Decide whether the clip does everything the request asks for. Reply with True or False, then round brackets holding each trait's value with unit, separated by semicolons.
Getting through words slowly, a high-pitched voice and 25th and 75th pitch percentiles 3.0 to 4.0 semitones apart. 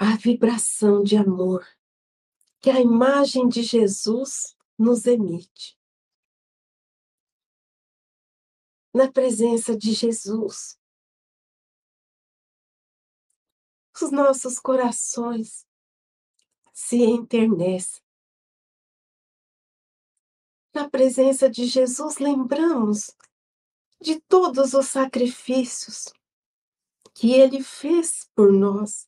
True (70 wpm; 245 Hz; 3.4 semitones)